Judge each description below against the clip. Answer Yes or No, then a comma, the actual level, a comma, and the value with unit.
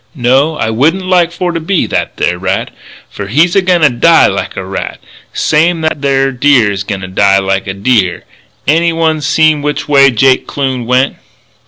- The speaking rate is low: No, average, 195 wpm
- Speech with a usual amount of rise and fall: No, wide, 6.3 semitones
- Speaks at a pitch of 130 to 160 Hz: Yes, medium, 140 Hz